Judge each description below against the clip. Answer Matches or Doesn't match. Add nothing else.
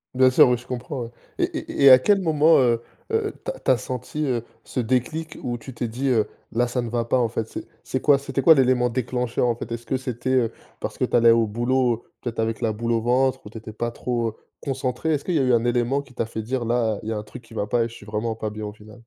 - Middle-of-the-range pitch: Doesn't match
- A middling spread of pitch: Doesn't match